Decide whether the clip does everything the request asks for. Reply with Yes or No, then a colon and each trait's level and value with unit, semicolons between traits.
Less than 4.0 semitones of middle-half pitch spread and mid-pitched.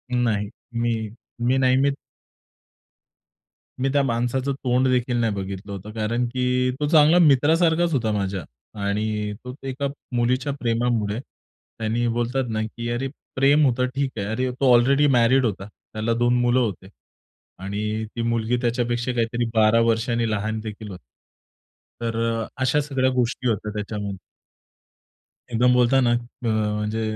No: average, 2.9 semitones; low, 120 Hz